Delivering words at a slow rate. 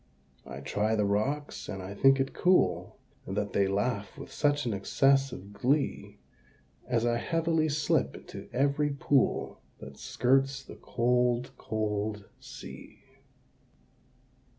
Yes: slow, 125 wpm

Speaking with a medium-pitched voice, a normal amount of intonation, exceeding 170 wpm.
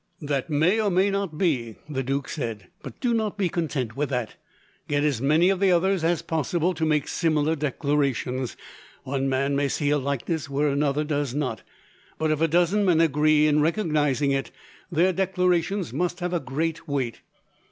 Yes: medium, 150 Hz; average, 3.8 semitones; average, 185 wpm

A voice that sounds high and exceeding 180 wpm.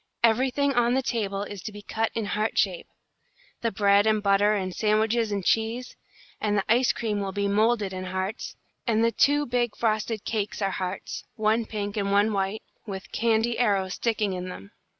Yes: high, 215 Hz; average, 190 wpm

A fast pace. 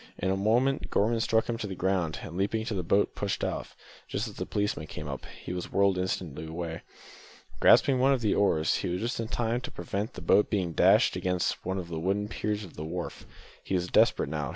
Yes: fast, 230 wpm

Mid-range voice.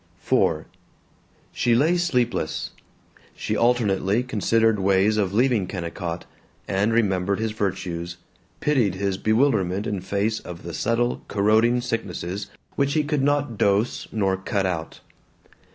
No: low, 105 Hz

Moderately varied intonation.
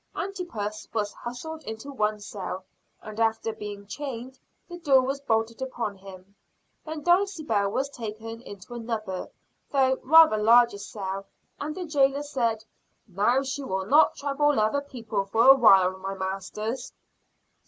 Yes: average, 5.0 semitones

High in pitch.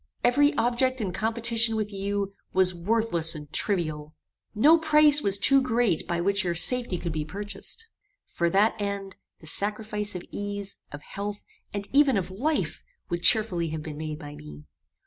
Yes: high, 200 Hz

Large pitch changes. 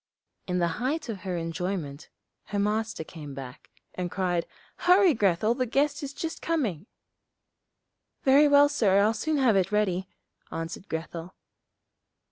Yes: wide, 7.7 semitones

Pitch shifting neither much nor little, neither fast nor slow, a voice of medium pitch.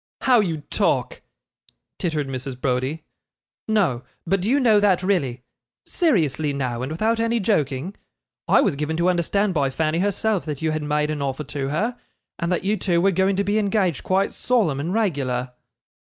No: wide, 6.0 semitones; average, 180 wpm; medium, 170 Hz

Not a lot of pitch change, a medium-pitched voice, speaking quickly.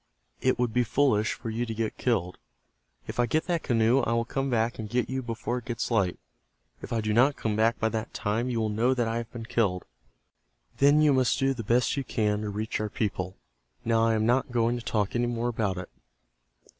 No: narrow, 2.1 semitones; low, 115 Hz; fast, 230 wpm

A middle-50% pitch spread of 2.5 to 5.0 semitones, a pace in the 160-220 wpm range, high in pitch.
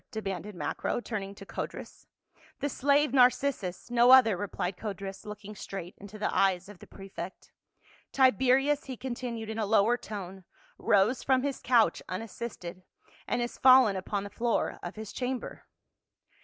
Yes: average, 4.3 semitones; average, 165 wpm; high, 215 Hz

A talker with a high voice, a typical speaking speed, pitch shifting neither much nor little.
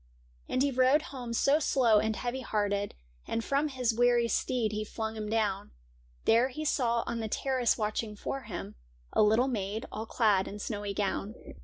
Yes: high, 225 Hz; average, 180 wpm; average, 3.3 semitones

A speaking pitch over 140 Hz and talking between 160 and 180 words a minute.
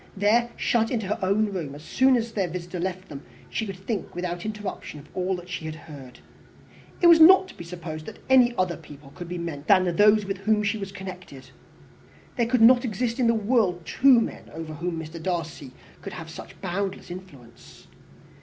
No: medium, 185 Hz; average, 200 wpm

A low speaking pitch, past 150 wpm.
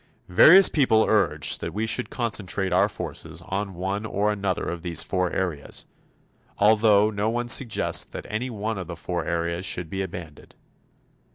Yes: low, 100 Hz; average, 160 wpm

